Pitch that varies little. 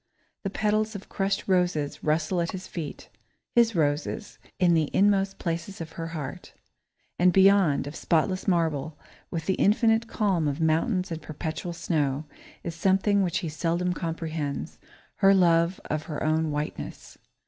No: average, 3.5 semitones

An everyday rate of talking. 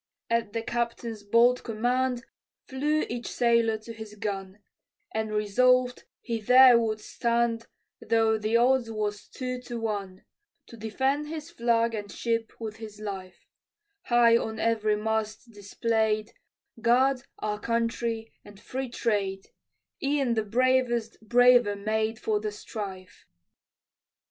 No: slow, 130 wpm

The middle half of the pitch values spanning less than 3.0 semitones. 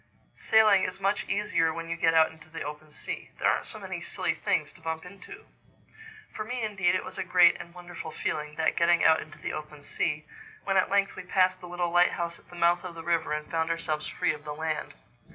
Yes: narrow, 2.5 semitones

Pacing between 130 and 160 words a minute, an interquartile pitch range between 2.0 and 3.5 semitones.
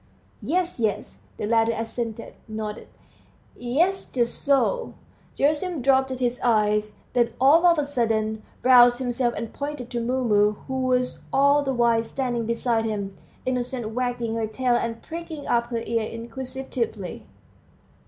Yes: average, 140 wpm; average, 2.7 semitones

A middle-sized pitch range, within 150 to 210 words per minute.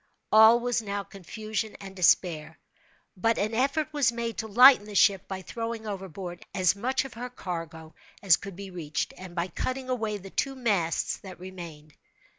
Yes: average, 4.2 semitones; average, 170 wpm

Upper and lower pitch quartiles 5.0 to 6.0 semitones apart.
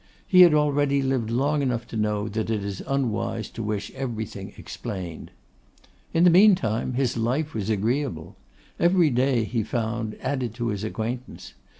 No: average, 4.2 semitones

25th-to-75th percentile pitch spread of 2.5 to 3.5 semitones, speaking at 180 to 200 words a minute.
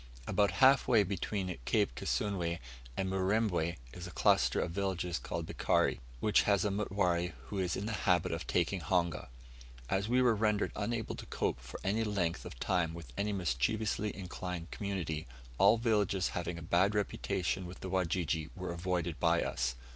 No: average, 3.0 semitones; average, 170 wpm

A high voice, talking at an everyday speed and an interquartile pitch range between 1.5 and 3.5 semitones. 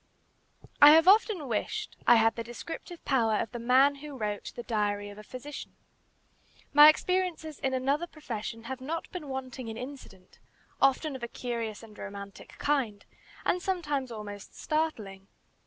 No: very high, 255 Hz; average, 155 wpm; average, 5.2 semitones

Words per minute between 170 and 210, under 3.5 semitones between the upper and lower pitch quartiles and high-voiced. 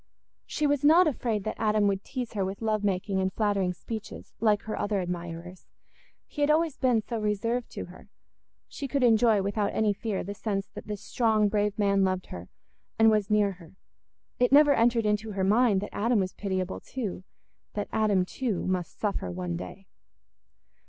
Yes: average, 180 wpm; average, 3.0 semitones; high, 210 Hz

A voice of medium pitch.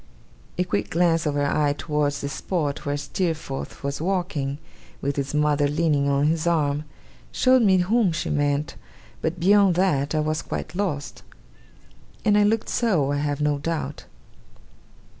Yes: medium, 150 Hz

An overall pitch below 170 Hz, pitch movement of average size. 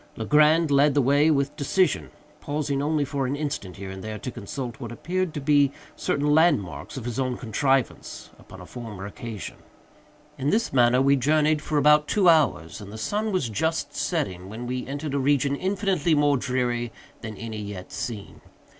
Yes: medium, 140 Hz; average, 4.2 semitones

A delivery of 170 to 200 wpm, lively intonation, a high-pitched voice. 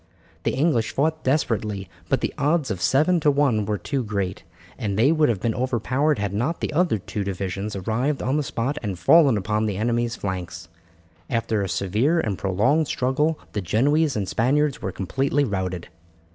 No: average, 180 wpm; wide, 6.4 semitones; low, 115 Hz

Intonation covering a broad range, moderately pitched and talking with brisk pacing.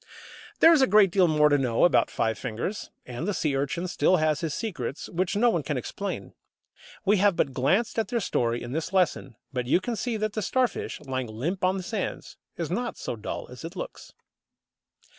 Yes: wide, 7.4 semitones; medium, 175 Hz; fast, 210 wpm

